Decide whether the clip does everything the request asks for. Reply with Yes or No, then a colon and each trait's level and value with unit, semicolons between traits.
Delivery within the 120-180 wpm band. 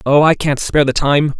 No: fast, 260 wpm